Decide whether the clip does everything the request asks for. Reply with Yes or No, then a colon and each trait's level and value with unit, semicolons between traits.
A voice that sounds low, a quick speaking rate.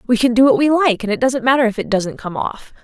No: high, 240 Hz; fast, 320 wpm